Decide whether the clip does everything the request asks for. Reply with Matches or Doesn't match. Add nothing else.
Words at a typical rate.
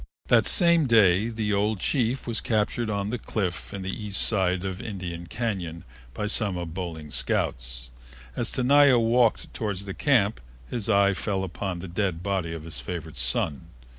Matches